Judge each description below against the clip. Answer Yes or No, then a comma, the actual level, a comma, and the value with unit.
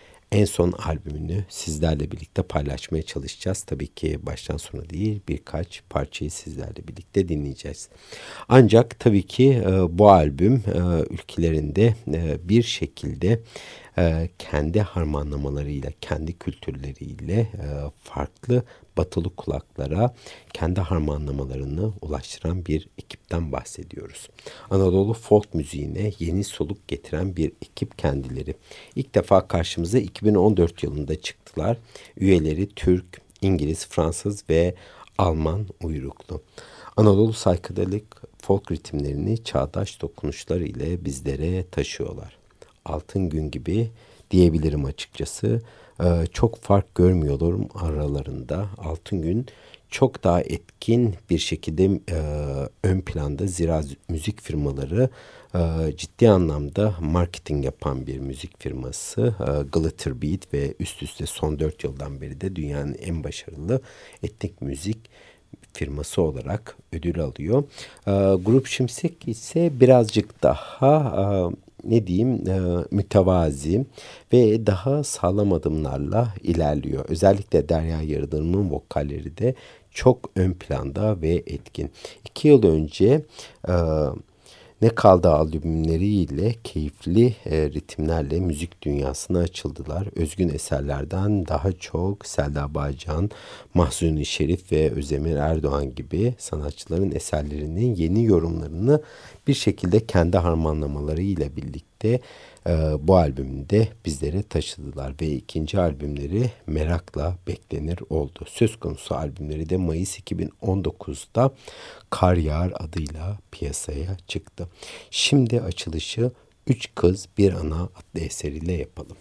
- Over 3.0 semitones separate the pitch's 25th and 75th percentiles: Yes, average, 5.1 semitones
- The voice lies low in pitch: Yes, very low, 85 Hz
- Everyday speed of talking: Yes, average, 105 wpm